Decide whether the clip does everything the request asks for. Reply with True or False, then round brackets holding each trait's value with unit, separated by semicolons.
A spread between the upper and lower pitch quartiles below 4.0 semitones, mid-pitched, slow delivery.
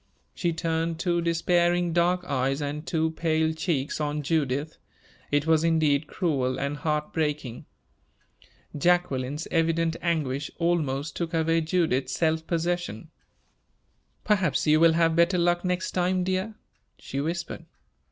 True (2.7 semitones; 160 Hz; 130 wpm)